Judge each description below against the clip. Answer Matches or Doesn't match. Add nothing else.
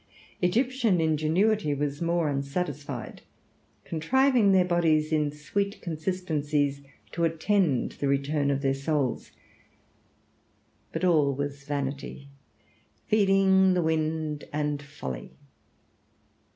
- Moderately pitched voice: Matches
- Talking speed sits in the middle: Doesn't match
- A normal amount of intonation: Matches